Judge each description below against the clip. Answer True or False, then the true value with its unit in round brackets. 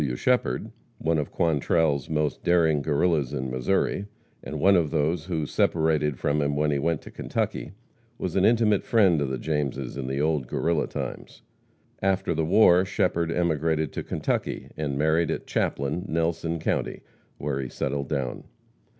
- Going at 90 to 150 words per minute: False (165 wpm)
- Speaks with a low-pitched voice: True (80 Hz)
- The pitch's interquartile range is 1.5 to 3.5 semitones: True (3.1 semitones)